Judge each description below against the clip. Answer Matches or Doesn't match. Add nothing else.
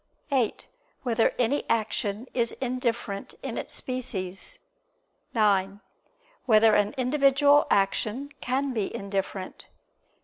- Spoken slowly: Matches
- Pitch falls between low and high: Doesn't match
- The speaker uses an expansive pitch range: Doesn't match